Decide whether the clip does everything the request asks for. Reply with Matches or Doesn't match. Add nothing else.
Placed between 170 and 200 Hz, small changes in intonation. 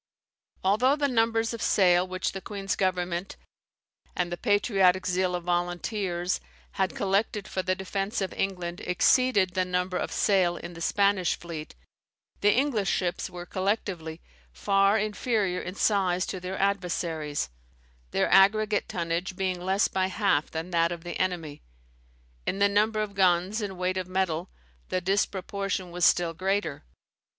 Matches